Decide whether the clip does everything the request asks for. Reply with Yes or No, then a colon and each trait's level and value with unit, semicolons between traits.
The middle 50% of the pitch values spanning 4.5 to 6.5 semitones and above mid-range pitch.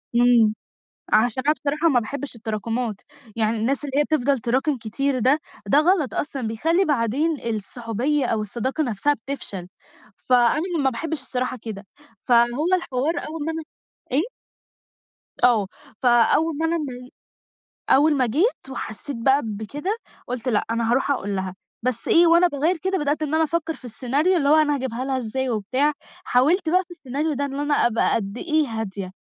Yes: average, 4.8 semitones; very high, 265 Hz